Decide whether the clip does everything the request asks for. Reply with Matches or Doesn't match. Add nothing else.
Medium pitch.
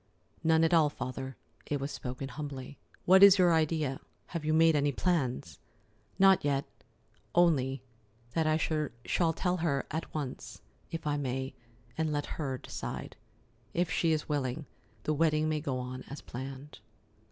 Matches